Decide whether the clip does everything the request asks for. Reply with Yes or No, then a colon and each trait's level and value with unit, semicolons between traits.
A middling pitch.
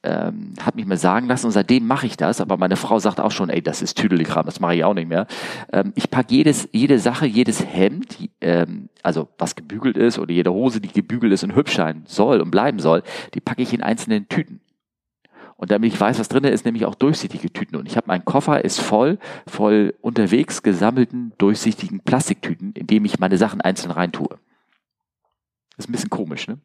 No: low, 115 Hz